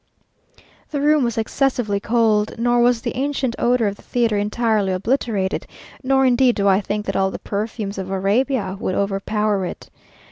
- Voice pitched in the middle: No, high, 220 Hz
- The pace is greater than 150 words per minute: Yes, average, 170 wpm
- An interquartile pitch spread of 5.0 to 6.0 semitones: No, average, 3.6 semitones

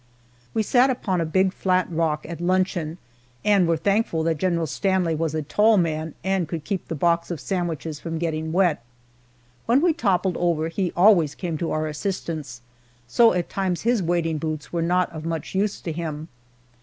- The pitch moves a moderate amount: Yes, average, 3.0 semitones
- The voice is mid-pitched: Yes, medium, 170 Hz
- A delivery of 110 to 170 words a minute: No, average, 185 wpm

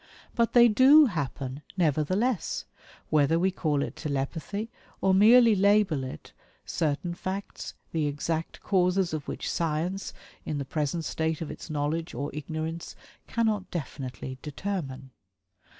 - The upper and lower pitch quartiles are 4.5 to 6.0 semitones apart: Yes, average, 4.8 semitones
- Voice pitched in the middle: Yes, medium, 165 Hz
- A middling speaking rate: No, slow, 130 wpm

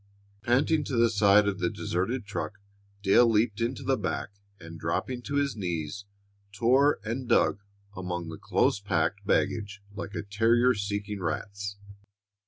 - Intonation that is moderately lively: Yes, average, 3.3 semitones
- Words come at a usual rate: Yes, average, 150 wpm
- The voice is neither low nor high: No, low, 105 Hz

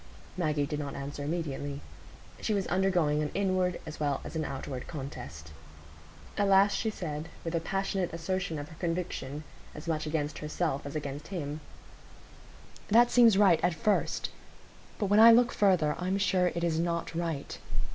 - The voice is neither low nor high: Yes, medium, 165 Hz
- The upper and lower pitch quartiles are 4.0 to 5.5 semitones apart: Yes, average, 4.3 semitones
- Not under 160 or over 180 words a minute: Yes, average, 165 wpm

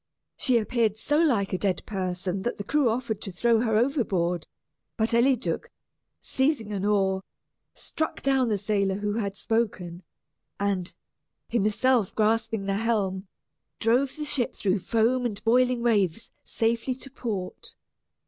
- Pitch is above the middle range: Yes, high, 220 Hz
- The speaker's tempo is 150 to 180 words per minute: No, average, 140 wpm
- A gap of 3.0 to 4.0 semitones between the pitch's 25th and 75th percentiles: Yes, average, 3.5 semitones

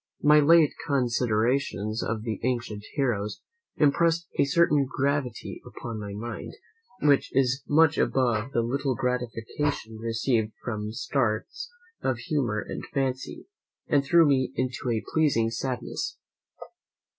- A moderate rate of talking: No, slow, 120 wpm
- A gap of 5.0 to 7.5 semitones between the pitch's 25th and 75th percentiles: No, average, 3.8 semitones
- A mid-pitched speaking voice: No, low, 125 Hz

